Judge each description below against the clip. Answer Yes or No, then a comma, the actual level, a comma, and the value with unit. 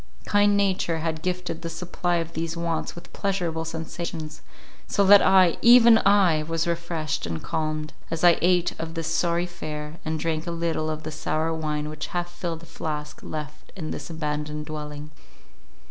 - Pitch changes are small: Yes, narrow, 2.1 semitones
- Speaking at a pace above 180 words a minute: No, average, 165 wpm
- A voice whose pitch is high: No, medium, 165 Hz